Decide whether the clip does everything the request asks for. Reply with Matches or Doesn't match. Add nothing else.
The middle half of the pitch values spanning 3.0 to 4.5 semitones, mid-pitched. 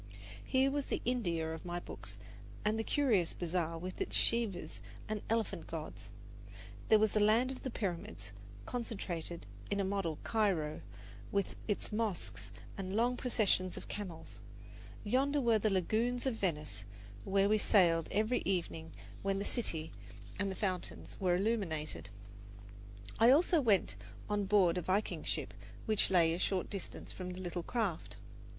Doesn't match